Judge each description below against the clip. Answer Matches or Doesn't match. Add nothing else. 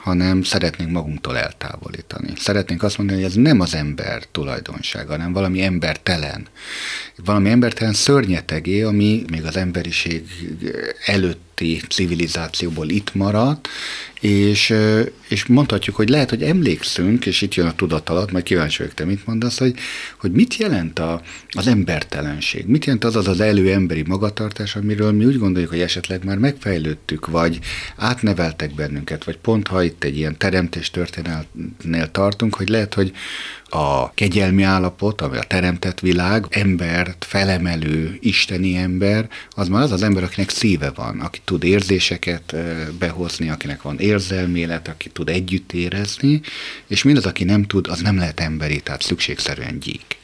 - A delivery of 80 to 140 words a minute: Doesn't match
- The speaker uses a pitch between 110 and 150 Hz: Doesn't match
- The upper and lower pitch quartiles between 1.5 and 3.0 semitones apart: Doesn't match